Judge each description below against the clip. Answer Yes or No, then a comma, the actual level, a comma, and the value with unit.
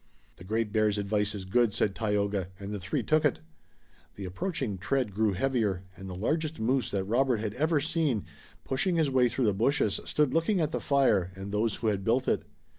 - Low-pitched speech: Yes, low, 110 Hz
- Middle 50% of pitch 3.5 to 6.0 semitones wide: Yes, average, 5.2 semitones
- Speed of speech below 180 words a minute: No, fast, 205 wpm